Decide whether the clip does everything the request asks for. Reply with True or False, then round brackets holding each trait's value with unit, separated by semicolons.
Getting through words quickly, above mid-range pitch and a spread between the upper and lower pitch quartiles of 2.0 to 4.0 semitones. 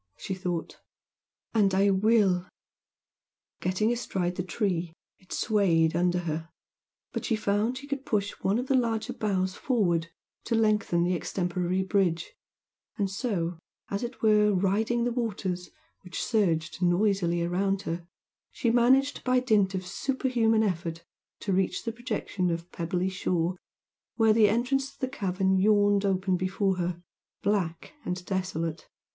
False (145 wpm; 195 Hz; 3.6 semitones)